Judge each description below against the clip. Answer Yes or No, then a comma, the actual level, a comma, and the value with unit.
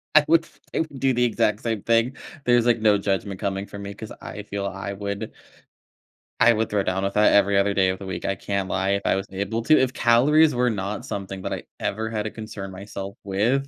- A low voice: Yes, low, 100 Hz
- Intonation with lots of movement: No, average, 3.0 semitones